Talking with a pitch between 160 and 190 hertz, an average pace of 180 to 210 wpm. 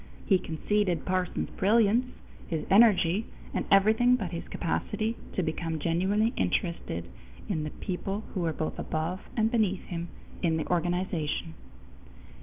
No: medium, 185 Hz; slow, 135 wpm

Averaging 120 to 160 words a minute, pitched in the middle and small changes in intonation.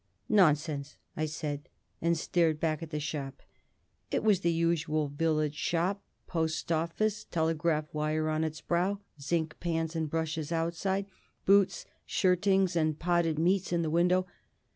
Yes: average, 140 wpm; medium, 165 Hz; narrow, 2.0 semitones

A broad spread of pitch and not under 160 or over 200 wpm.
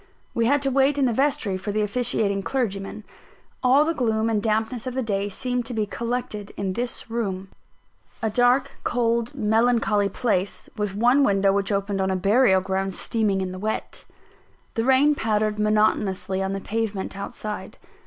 No: average, 3.6 semitones; average, 175 wpm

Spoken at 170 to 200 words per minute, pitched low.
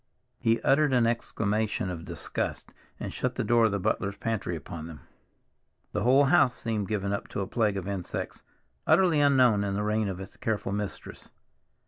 Yes: average, 180 wpm; low, 105 Hz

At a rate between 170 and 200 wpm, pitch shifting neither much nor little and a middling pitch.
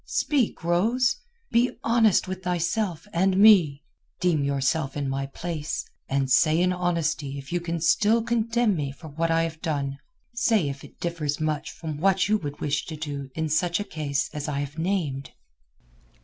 Yes: average, 175 wpm; average, 4.7 semitones; medium, 165 Hz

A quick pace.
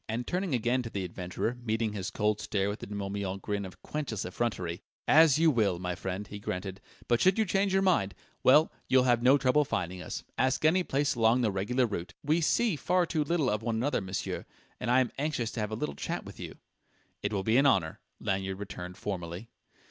Yes: fast, 225 wpm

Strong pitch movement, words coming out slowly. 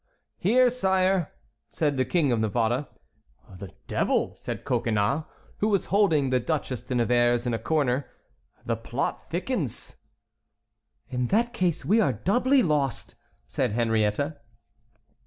Yes: wide, 7.8 semitones; slow, 130 wpm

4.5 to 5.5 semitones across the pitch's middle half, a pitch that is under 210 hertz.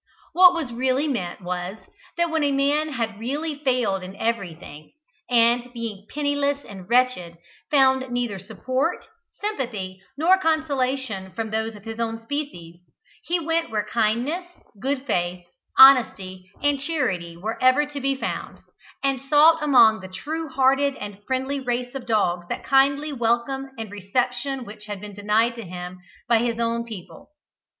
No: average, 5.2 semitones; high, 245 Hz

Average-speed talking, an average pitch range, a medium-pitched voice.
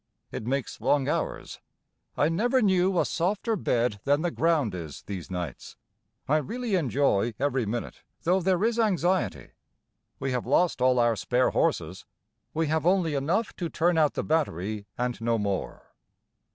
No: average, 160 wpm; wide, 7.1 semitones; medium, 145 Hz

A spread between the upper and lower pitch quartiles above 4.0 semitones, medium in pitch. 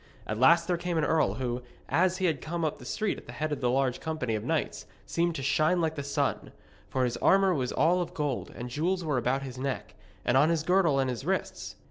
Yes: average, 4.8 semitones; medium, 150 Hz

